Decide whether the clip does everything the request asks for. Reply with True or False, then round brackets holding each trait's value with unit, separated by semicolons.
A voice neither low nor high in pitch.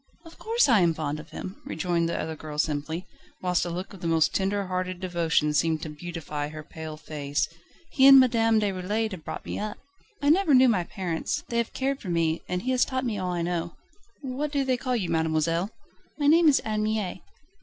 True (180 Hz)